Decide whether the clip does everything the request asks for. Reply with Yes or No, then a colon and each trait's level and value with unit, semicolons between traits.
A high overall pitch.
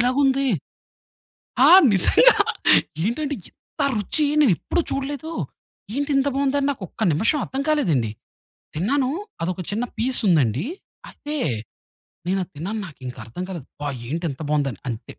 Yes: high, 215 Hz